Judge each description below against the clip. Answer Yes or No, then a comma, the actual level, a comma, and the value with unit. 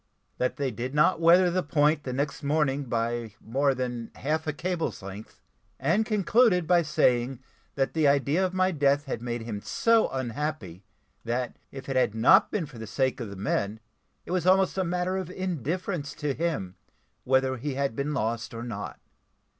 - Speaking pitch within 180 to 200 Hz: No, medium, 140 Hz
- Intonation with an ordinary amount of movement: No, wide, 5.9 semitones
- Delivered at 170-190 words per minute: Yes, average, 185 wpm